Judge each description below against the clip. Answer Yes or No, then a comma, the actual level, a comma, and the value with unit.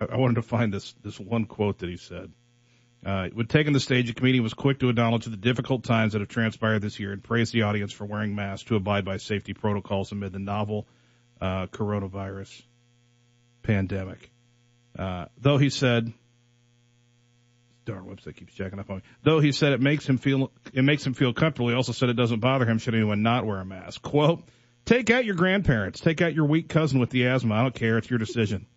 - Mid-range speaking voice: No, low, 120 Hz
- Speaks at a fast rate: Yes, fast, 215 wpm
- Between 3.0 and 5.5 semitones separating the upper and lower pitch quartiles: Yes, average, 3.4 semitones